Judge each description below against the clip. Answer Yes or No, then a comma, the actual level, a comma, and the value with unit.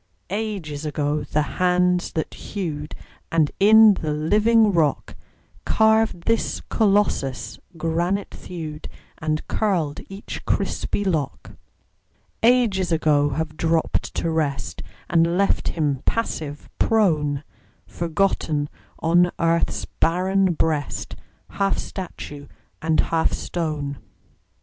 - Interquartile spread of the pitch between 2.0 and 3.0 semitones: No, average, 4.3 semitones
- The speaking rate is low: Yes, slow, 100 wpm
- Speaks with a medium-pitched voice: Yes, medium, 165 Hz